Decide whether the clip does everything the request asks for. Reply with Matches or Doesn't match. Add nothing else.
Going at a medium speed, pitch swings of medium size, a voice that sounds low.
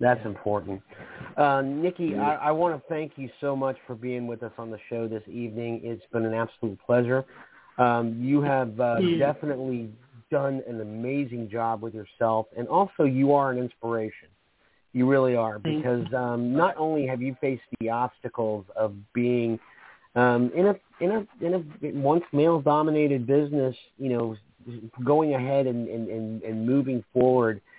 Matches